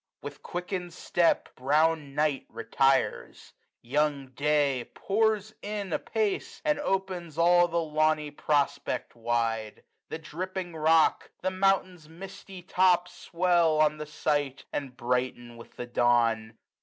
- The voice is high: No, medium, 155 Hz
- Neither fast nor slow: No, slow, 120 wpm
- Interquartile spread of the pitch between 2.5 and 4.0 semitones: No, average, 4.8 semitones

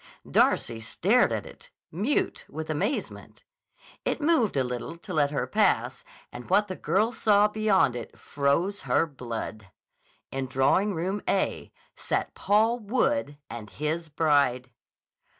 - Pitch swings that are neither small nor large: No, wide, 7.7 semitones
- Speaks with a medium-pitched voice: Yes, medium, 160 Hz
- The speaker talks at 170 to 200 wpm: No, slow, 135 wpm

